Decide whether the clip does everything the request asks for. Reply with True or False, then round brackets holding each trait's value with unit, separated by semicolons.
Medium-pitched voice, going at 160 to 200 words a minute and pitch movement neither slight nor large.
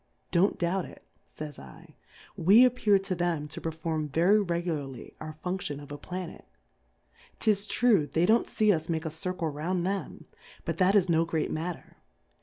True (170 Hz; 180 wpm; 3.6 semitones)